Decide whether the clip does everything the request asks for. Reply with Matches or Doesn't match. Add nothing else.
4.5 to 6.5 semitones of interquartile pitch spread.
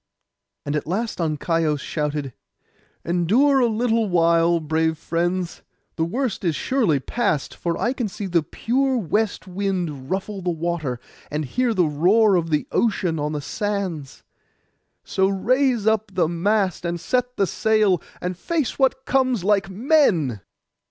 Matches